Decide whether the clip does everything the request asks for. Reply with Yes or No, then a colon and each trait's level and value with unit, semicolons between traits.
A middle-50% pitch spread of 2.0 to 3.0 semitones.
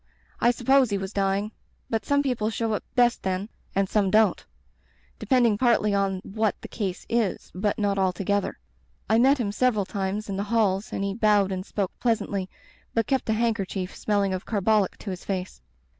Yes: average, 2.7 semitones